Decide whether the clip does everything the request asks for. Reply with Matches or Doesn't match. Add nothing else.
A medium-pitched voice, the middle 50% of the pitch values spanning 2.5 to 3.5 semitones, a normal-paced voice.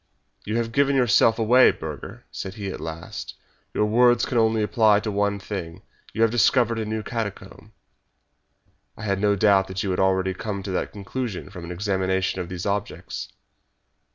Doesn't match